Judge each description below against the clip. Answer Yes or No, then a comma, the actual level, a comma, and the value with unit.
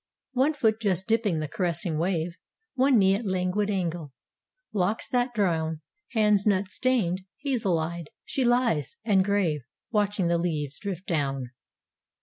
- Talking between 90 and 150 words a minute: Yes, average, 140 wpm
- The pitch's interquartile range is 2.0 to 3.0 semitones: No, average, 4.5 semitones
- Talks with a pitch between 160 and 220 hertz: Yes, high, 190 Hz